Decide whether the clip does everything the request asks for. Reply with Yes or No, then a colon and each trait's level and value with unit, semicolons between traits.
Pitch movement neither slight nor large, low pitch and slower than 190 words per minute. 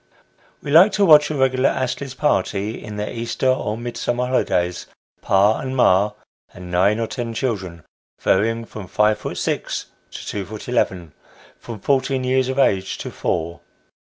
Yes: average, 4.8 semitones; low, 115 Hz; average, 165 wpm